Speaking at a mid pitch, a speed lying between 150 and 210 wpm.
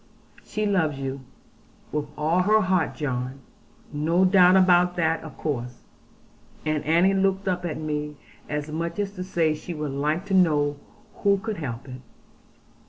Yes: medium, 160 Hz; average, 160 wpm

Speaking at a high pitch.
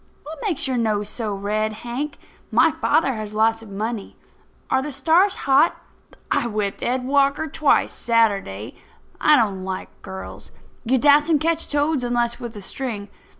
Yes: high, 240 Hz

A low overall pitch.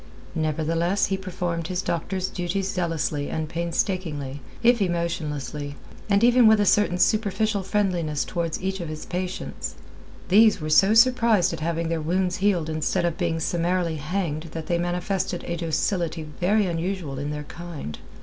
No: medium, 175 Hz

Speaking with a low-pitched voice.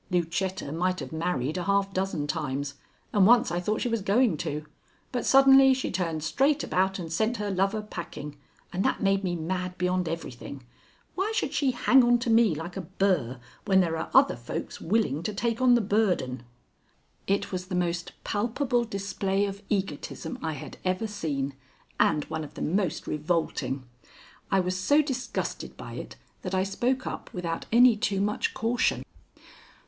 No: high, 190 Hz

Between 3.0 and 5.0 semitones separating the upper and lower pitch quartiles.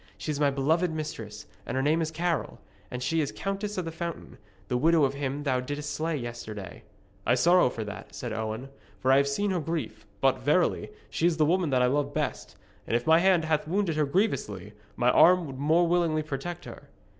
Yes: average, 4.6 semitones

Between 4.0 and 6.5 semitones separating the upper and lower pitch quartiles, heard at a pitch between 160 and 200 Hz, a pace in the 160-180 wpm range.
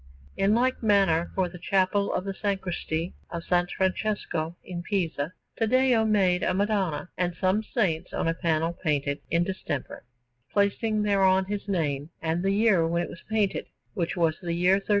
No: average, 3.2 semitones; medium, 185 Hz; average, 170 wpm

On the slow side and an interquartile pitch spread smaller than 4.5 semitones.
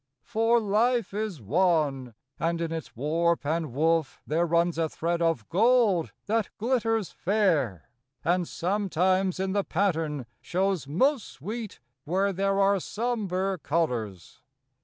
Yes: slow, 130 wpm; average, 4.1 semitones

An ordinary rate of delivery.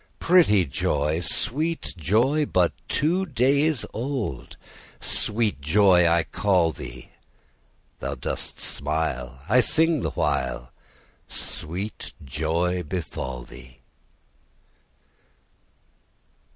No: slow, 85 wpm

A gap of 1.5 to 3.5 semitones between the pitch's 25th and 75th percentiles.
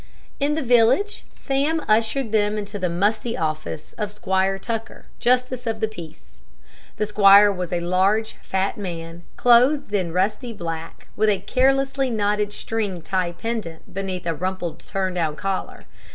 No: average, 4.1 semitones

